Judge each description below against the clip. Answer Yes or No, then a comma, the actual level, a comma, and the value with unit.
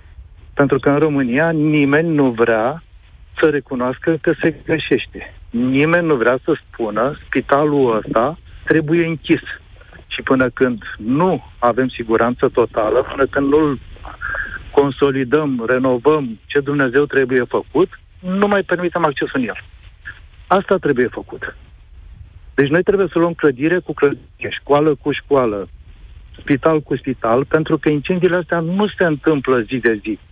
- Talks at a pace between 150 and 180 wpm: No, average, 140 wpm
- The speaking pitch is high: No, medium, 140 Hz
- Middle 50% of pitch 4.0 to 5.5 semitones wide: Yes, average, 4.6 semitones